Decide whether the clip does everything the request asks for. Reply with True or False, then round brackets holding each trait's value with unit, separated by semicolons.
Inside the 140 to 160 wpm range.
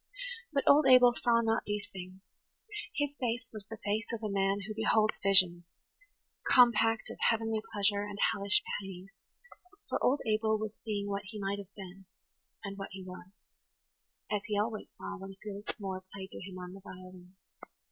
False (170 wpm)